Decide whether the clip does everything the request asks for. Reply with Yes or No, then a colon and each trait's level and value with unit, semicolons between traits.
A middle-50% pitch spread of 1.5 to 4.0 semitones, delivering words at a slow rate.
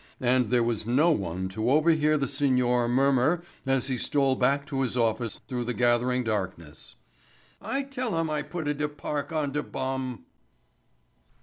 No: average, 3.5 semitones; average, 165 wpm